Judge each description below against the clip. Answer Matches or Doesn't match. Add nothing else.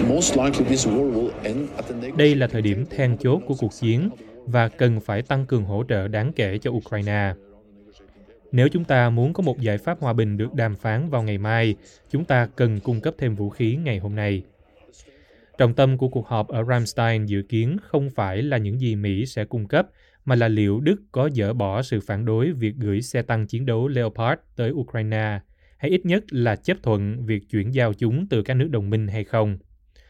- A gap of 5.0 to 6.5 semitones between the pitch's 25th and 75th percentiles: Doesn't match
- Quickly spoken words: Doesn't match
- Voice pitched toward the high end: Doesn't match